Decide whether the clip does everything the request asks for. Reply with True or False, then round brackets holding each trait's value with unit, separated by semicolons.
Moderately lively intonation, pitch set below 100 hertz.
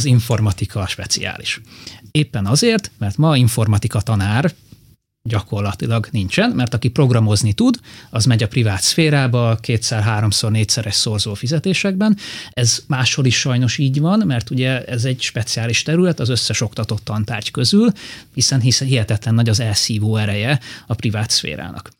False (3.3 semitones; 120 Hz)